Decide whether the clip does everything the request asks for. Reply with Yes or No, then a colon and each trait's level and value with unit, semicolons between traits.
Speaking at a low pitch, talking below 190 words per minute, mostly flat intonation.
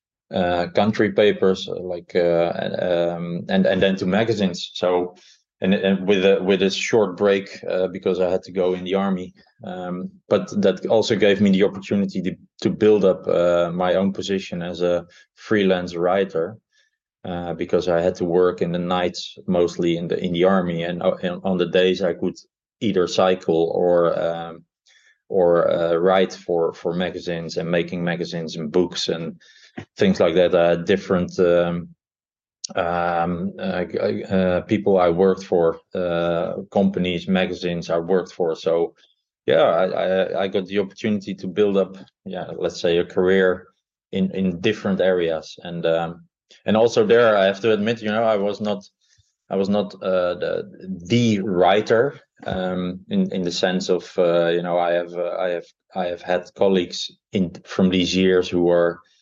Yes: very low, 90 Hz; average, 170 wpm; narrow, 1.9 semitones